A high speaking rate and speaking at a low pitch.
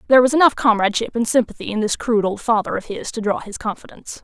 No: fast, 240 wpm; high, 230 Hz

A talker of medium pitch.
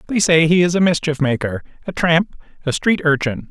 Yes: medium, 160 Hz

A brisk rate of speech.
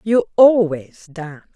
No: slow, 115 wpm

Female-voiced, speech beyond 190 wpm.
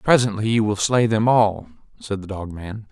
No: male; fast, 205 wpm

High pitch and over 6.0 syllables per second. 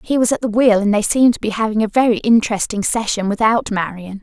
Yes: high, 220 Hz; 6.3 syllables/s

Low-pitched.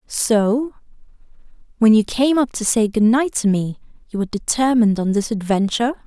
No: high, 225 Hz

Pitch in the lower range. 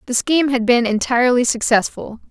No: high, 245 Hz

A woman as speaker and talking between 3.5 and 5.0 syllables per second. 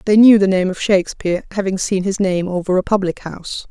No: female; 6.1 syllables/s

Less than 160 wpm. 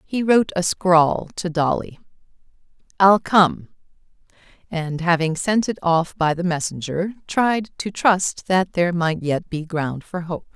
Yes: average, 150 wpm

